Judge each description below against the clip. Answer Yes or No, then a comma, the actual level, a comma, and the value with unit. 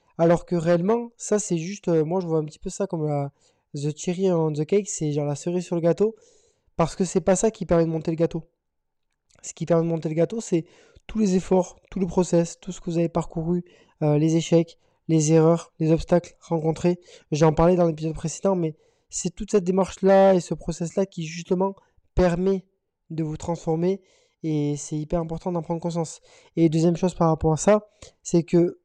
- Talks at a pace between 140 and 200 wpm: No, average, 210 wpm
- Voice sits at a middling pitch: Yes, medium, 170 Hz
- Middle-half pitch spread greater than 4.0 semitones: No, narrow, 2.5 semitones